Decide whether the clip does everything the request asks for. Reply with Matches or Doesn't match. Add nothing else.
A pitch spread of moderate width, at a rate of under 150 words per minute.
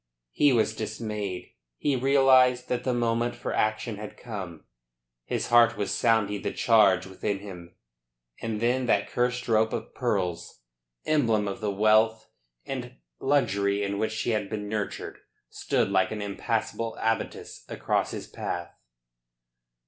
Matches